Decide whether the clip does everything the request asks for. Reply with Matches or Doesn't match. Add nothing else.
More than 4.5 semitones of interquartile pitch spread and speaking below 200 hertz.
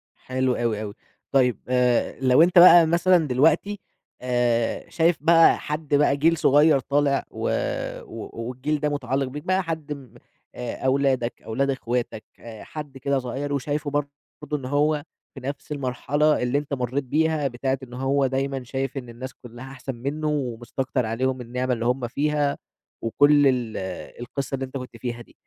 Doesn't match